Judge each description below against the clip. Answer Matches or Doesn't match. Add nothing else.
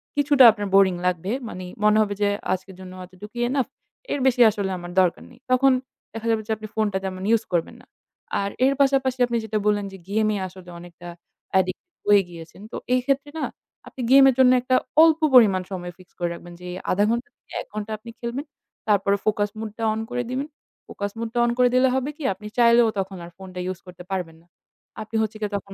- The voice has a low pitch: Doesn't match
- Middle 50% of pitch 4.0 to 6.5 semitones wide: Matches